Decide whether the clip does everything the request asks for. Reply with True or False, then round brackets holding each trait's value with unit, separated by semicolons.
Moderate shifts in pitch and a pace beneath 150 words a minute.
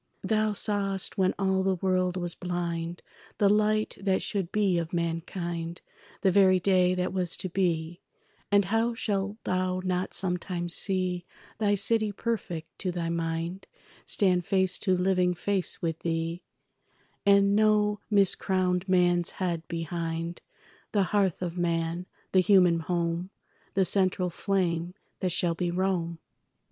False (2.3 semitones; 140 wpm)